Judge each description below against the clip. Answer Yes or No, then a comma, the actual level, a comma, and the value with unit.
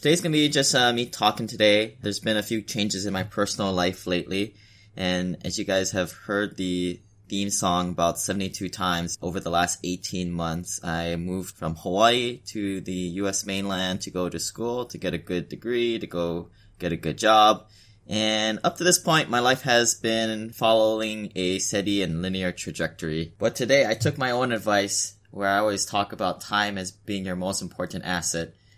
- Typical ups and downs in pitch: Yes, average, 3.4 semitones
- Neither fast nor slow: Yes, average, 190 wpm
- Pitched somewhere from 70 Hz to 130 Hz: Yes, low, 100 Hz